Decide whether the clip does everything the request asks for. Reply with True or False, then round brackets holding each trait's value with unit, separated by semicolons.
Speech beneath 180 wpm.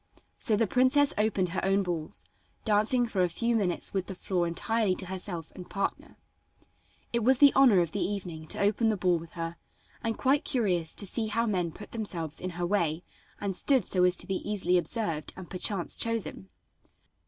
False (195 wpm)